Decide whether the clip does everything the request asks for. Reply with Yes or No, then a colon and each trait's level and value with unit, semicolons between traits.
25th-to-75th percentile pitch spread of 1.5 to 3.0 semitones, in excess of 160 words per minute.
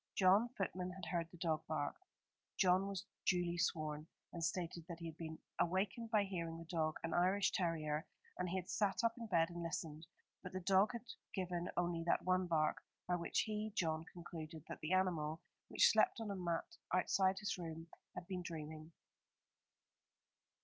Yes: narrow, 2.4 semitones; average, 180 wpm